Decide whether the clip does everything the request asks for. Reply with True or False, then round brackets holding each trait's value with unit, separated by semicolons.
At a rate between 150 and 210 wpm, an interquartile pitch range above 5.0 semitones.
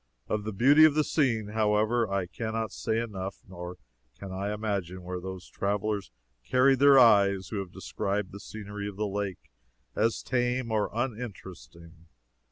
False (165 wpm; 3.3 semitones)